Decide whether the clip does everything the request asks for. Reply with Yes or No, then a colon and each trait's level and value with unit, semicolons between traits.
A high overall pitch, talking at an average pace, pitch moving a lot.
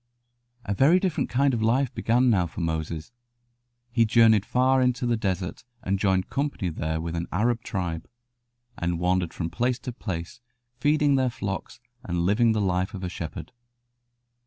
No: low, 105 Hz; average, 165 wpm; wide, 5.9 semitones